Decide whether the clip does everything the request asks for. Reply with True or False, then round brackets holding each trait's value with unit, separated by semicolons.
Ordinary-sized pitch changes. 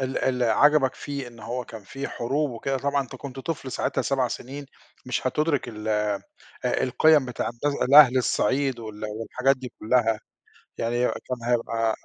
True (3.0 semitones)